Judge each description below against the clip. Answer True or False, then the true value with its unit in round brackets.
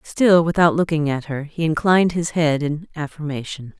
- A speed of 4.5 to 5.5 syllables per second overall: True (5.0 syllables/s)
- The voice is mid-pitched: True (160 Hz)